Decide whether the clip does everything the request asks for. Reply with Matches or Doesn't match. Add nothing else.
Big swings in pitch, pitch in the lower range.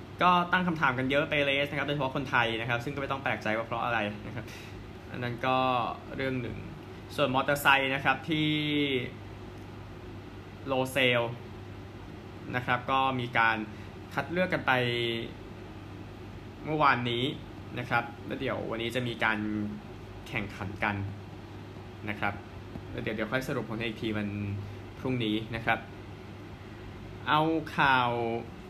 Doesn't match